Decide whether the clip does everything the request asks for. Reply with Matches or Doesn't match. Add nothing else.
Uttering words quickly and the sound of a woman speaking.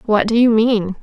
Matches